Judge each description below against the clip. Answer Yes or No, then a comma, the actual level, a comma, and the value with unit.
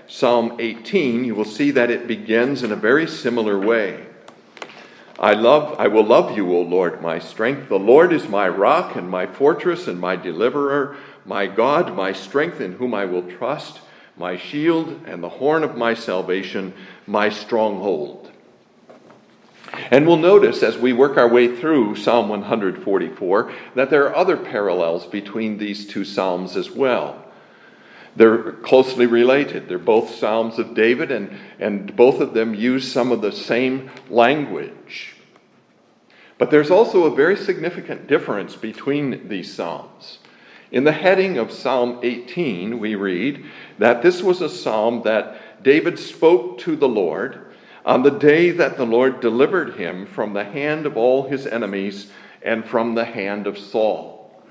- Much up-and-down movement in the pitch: No, average, 4.5 semitones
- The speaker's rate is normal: Yes, average, 160 wpm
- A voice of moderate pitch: No, low, 120 Hz